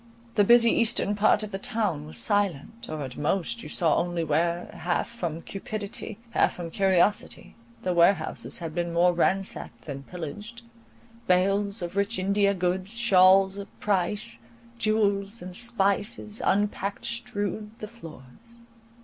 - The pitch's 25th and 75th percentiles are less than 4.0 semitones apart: Yes, average, 3.4 semitones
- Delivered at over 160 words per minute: No, average, 140 wpm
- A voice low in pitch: No, high, 195 Hz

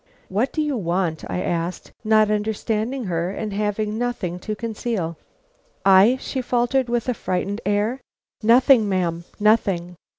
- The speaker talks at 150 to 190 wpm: No, average, 140 wpm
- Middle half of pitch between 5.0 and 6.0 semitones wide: No, average, 4.3 semitones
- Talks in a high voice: Yes, high, 210 Hz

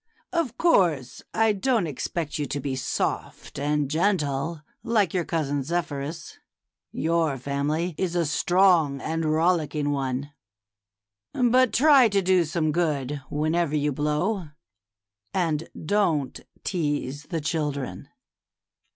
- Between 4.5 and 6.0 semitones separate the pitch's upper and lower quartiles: No, average, 3.8 semitones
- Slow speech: Yes, slow, 115 wpm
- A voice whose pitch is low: No, medium, 160 Hz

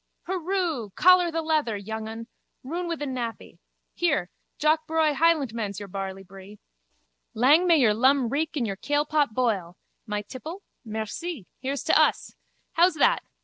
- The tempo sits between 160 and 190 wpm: No, average, 145 wpm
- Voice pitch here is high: Yes, very high, 275 Hz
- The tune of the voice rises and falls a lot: Yes, wide, 6.9 semitones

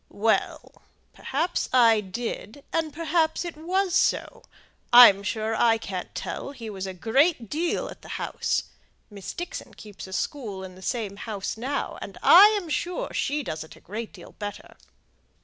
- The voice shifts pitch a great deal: Yes, wide, 7.5 semitones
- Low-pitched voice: No, high, 235 Hz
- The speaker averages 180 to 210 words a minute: No, average, 165 wpm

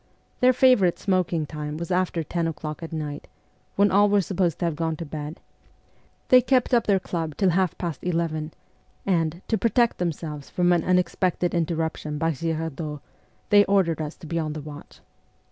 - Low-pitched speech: No, medium, 170 Hz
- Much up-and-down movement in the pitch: No, average, 3.1 semitones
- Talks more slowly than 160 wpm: No, average, 180 wpm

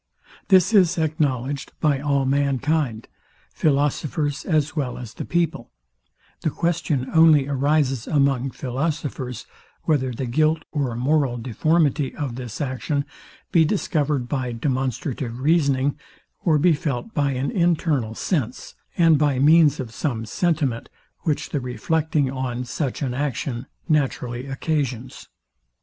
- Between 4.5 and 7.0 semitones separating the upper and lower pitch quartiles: No, average, 3.4 semitones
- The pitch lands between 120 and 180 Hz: Yes, medium, 140 Hz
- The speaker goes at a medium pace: No, slow, 125 wpm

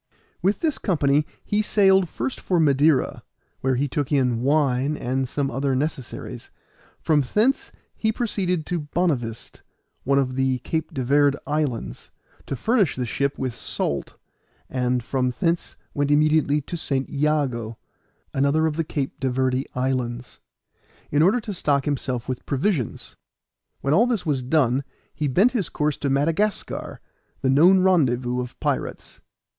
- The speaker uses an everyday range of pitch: Yes, average, 4.0 semitones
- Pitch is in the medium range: Yes, medium, 145 Hz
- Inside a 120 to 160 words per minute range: Yes, average, 150 wpm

